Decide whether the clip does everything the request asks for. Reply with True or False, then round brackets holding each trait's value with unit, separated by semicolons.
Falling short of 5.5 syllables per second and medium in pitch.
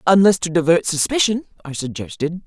False (5.7 syllables/s; 170 Hz)